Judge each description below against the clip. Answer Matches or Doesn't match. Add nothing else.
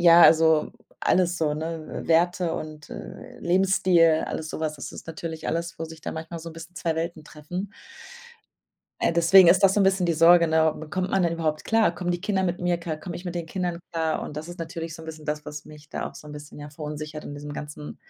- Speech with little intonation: Matches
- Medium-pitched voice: Matches